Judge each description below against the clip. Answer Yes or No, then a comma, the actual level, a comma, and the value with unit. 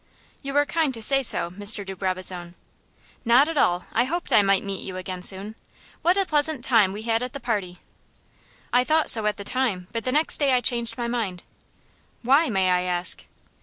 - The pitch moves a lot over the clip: Yes, wide, 6.0 semitones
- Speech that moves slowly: No, fast, 205 wpm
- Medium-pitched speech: No, high, 225 Hz